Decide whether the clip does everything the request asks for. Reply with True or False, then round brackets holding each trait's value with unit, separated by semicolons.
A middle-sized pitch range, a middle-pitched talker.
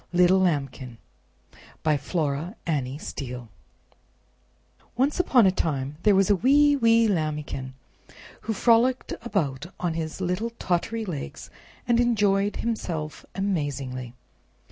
False (7.6 semitones; 180 Hz)